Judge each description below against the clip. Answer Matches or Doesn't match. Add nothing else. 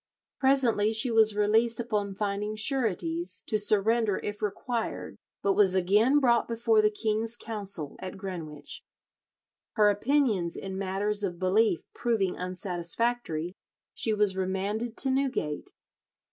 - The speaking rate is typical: Doesn't match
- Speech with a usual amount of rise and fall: Matches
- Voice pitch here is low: Doesn't match